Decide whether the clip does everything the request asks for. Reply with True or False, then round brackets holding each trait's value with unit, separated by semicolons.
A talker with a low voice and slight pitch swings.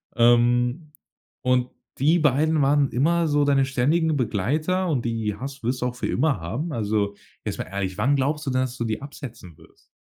False (130 Hz; 3.9 semitones)